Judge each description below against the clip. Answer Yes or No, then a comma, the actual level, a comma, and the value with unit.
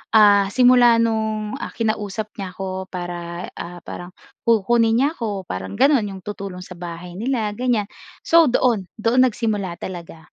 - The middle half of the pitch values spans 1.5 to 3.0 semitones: No, average, 4.1 semitones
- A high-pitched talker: Yes, high, 210 Hz